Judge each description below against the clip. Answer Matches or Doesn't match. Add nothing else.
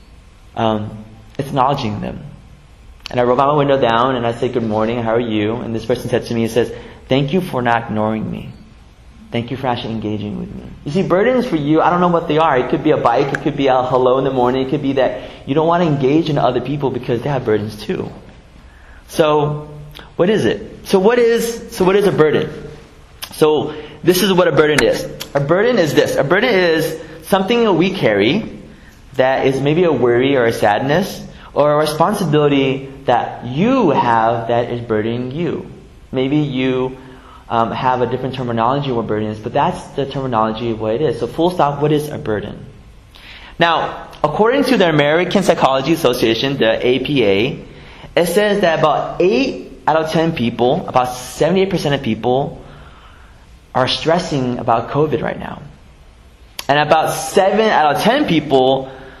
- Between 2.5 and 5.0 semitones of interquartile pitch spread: Doesn't match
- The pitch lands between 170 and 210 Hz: Doesn't match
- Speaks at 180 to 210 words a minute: Matches